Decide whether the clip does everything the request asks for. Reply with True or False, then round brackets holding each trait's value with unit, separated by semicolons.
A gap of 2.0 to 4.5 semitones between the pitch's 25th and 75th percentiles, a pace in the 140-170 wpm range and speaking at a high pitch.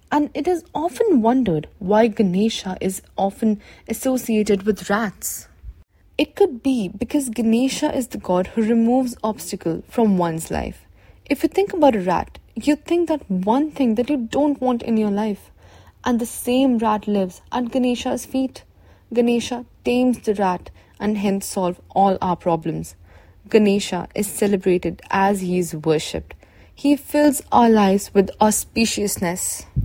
False (5.2 semitones; 150 wpm; 220 Hz)